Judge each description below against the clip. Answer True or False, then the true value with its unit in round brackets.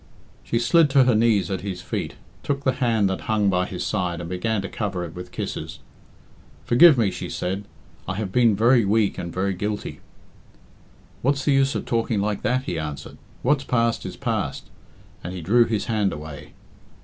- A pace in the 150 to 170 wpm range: False (190 wpm)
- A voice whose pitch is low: True (105 Hz)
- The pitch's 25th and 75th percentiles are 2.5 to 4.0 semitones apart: False (4.5 semitones)